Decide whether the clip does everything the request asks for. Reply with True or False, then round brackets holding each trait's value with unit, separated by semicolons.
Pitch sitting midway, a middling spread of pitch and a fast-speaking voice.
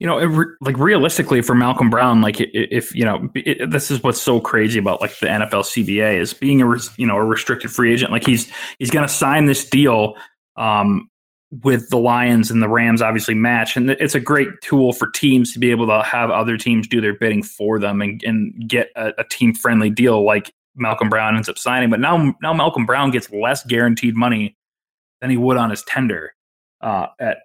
False (120 Hz; 3.1 semitones; 220 wpm)